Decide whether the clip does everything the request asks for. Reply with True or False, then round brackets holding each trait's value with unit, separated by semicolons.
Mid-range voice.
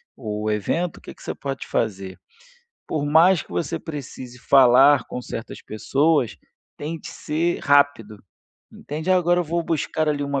True (145 Hz)